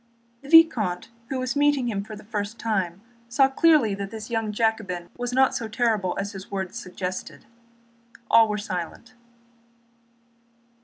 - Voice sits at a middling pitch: No, high, 220 Hz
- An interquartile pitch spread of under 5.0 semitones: Yes, average, 3.7 semitones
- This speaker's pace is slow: No, average, 150 wpm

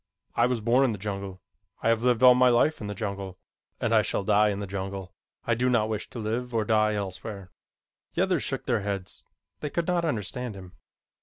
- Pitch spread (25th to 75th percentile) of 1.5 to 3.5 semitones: No, average, 3.9 semitones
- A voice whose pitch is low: Yes, low, 110 Hz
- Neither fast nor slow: No, fast, 220 wpm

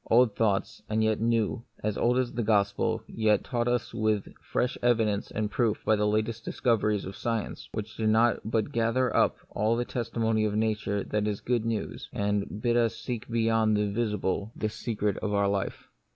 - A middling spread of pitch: No, narrow, 1.8 semitones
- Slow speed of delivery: No, average, 185 wpm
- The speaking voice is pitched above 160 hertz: No, low, 110 Hz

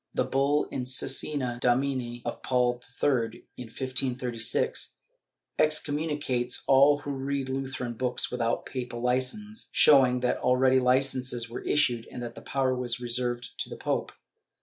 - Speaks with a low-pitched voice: Yes, low, 125 Hz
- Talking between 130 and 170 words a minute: Yes, average, 145 wpm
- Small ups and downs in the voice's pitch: Yes, narrow, 1.9 semitones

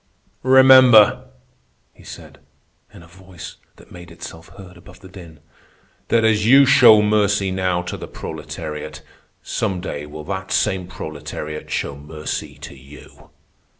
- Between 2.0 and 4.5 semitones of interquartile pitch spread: No, average, 5.2 semitones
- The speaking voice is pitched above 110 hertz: No, very low, 90 Hz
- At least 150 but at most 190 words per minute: No, average, 140 wpm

